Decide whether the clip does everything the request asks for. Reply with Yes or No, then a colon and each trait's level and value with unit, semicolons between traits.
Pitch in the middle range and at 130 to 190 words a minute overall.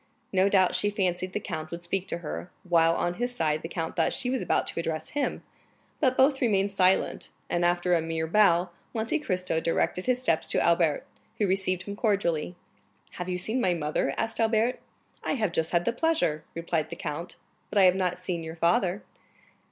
No: medium, 180 Hz; average, 200 wpm